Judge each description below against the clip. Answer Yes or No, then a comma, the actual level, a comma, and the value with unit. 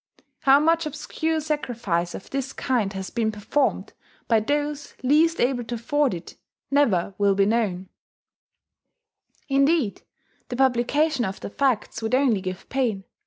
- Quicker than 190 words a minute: No, average, 140 wpm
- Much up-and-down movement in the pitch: Yes, wide, 5.8 semitones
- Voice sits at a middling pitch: No, very high, 250 Hz